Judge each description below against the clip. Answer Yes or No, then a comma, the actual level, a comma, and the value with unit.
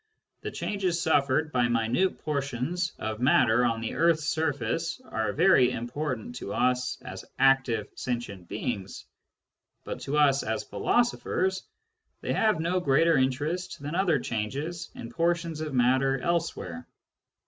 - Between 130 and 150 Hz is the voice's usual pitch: Yes, medium, 140 Hz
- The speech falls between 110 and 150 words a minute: Yes, slow, 135 wpm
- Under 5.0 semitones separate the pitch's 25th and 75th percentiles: No, wide, 5.6 semitones